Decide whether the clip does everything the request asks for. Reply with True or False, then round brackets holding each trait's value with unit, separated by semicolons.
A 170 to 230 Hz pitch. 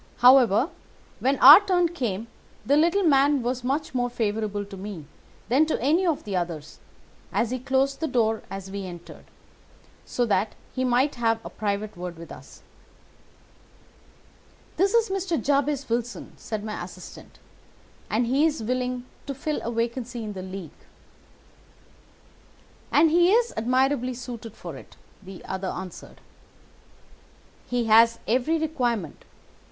False (245 Hz)